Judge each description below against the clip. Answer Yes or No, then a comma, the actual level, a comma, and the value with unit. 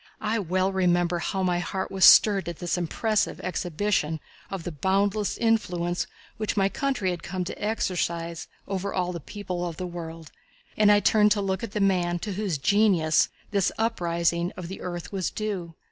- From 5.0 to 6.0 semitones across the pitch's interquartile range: No, average, 2.9 semitones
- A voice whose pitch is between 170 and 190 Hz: Yes, medium, 185 Hz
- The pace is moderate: Yes, average, 180 wpm